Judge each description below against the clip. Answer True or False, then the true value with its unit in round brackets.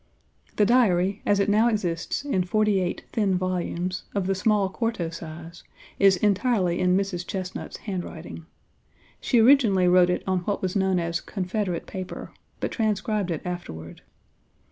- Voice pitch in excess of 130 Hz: True (185 Hz)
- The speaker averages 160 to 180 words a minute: False (150 wpm)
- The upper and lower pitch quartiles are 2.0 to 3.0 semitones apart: True (2.7 semitones)